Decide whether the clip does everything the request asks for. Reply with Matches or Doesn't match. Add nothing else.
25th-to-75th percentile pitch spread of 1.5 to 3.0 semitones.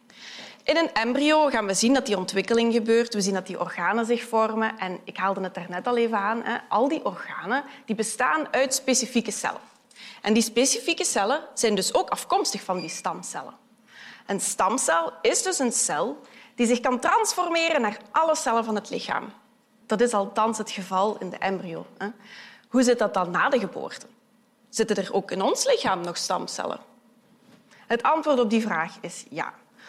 Doesn't match